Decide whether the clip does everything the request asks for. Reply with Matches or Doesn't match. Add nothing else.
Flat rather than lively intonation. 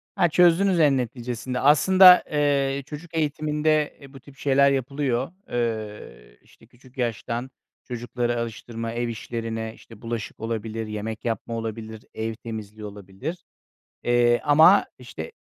Doesn't match